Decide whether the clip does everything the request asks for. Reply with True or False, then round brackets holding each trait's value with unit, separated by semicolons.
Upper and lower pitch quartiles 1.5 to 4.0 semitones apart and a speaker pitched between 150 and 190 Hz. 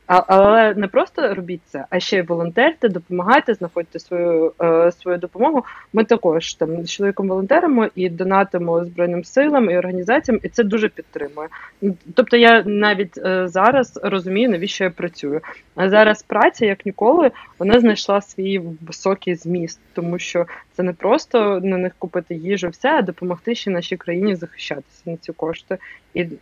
True (3.2 semitones; 185 Hz)